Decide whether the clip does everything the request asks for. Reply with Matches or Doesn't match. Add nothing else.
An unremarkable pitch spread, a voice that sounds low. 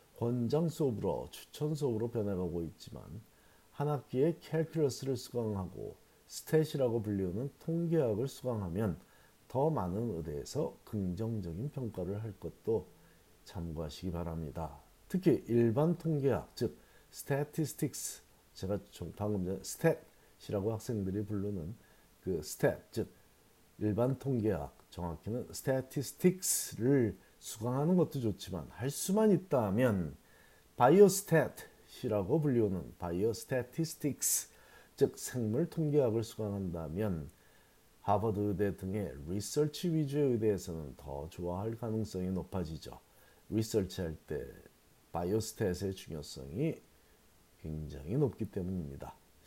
Doesn't match